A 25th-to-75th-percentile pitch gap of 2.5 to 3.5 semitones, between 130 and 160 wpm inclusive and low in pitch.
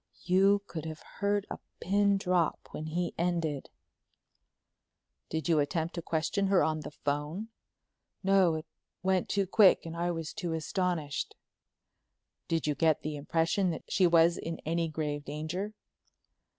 No: average, 3.1 semitones; average, 150 wpm; medium, 170 Hz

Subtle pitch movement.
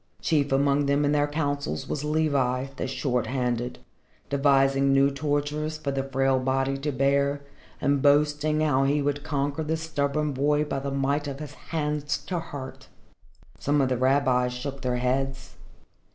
Yes: narrow, 1.6 semitones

